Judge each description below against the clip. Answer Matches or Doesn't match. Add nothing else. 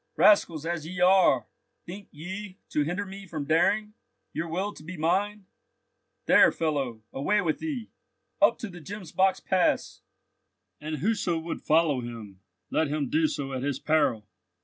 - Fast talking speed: Doesn't match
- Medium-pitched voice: Matches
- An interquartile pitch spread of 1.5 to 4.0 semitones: Doesn't match